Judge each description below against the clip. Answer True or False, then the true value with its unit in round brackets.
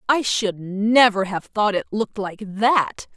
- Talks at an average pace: True (170 wpm)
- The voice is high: True (210 Hz)